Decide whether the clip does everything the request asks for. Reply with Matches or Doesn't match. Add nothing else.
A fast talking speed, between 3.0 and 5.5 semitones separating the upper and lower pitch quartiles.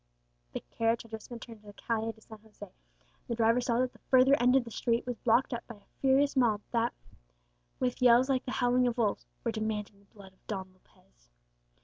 Doesn't match